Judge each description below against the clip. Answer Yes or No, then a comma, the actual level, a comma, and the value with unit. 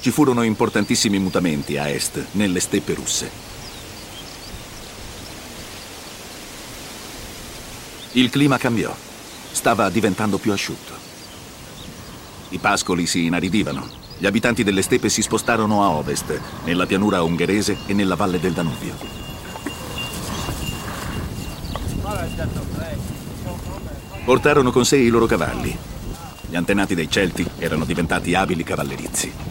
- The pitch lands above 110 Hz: No, low, 100 Hz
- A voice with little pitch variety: No, average, 4.7 semitones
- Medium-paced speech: No, slow, 100 wpm